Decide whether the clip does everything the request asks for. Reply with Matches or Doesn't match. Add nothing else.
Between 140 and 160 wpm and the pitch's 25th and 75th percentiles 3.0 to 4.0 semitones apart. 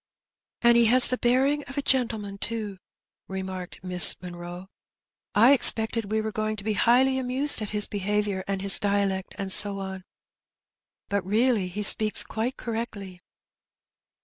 Matches